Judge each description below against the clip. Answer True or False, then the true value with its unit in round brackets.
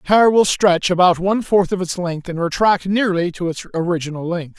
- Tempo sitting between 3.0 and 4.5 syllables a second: False (5.3 syllables/s)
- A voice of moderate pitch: True (180 Hz)